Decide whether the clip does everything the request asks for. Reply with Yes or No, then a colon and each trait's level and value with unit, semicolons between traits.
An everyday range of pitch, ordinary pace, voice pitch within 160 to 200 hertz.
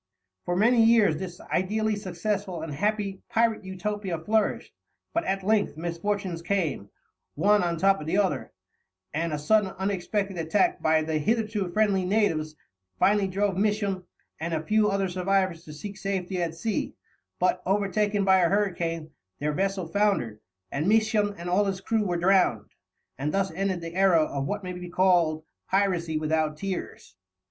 Yes: average, 3.5 semitones; average, 165 wpm; high, 190 Hz